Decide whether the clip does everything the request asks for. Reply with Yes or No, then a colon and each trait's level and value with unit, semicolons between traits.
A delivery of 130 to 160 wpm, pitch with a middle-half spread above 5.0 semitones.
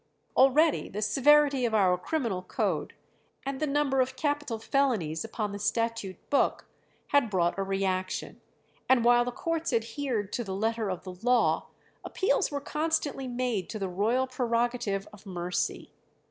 Yes: average, 155 wpm; wide, 5.5 semitones